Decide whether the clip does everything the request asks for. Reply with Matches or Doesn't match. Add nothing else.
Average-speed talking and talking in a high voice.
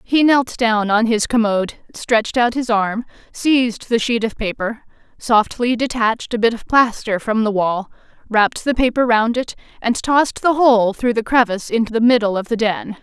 Matches